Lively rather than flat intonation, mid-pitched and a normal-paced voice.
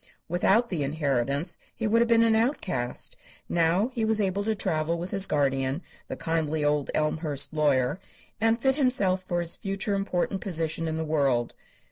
Yes: wide, 5.8 semitones; medium, 170 Hz; average, 170 wpm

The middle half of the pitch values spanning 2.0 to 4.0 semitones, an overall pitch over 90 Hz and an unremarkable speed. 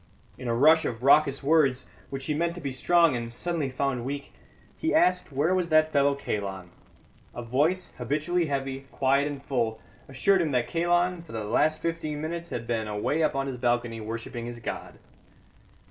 No: average, 5.0 semitones; medium, 140 Hz; average, 185 wpm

